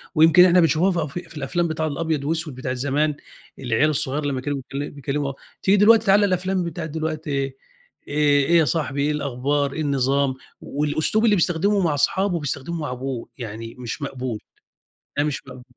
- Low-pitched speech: No, medium, 150 Hz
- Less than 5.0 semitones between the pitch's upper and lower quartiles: Yes, average, 3.5 semitones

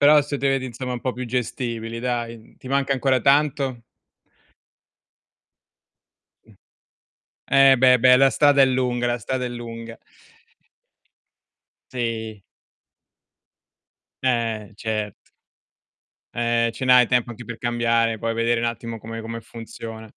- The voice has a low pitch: Yes, low, 120 Hz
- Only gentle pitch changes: Yes, narrow, 2.1 semitones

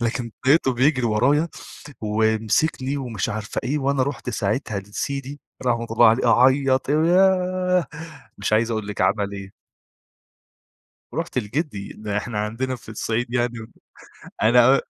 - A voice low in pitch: Yes, low, 120 Hz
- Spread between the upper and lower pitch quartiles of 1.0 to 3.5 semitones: No, average, 4.3 semitones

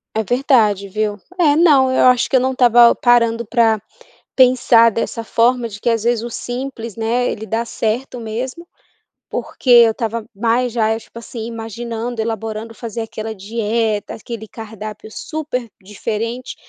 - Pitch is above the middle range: Yes, high, 230 Hz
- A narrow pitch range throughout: Yes, narrow, 1.9 semitones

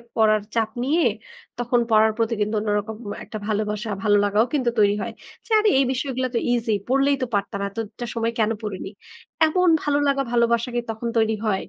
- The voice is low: No, high, 225 Hz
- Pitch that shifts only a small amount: No, average, 3.2 semitones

